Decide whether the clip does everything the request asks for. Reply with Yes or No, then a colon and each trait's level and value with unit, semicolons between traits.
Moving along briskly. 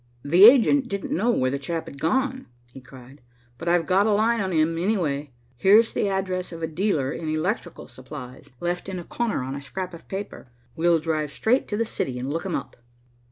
Yes: fast, 210 wpm